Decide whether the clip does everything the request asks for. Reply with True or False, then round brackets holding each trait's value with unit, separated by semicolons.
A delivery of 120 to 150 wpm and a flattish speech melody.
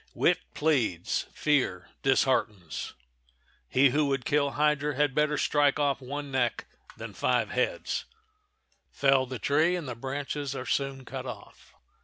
True (135 wpm; 2.3 semitones)